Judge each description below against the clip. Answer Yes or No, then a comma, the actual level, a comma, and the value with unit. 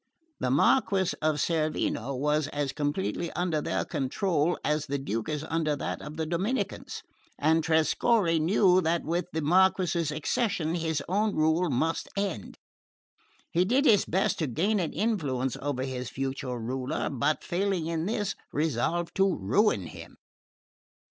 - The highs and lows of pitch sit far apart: No, average, 4.1 semitones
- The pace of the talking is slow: No, average, 150 wpm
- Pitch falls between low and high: Yes, medium, 160 Hz